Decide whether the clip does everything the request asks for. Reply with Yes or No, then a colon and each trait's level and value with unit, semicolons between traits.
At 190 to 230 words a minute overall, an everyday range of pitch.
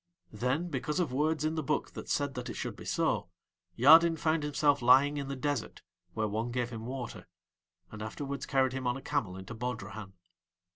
Yes: average, 195 wpm; average, 3.6 semitones